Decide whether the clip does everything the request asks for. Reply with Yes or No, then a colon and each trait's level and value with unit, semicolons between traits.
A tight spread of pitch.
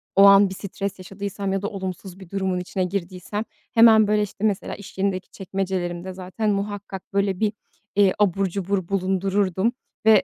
Yes: narrow, 1.5 semitones